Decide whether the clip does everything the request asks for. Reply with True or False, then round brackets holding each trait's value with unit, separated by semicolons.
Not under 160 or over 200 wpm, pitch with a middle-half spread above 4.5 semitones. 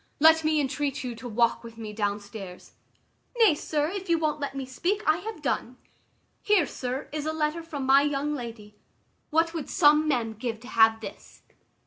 True (190 wpm; 5.1 semitones)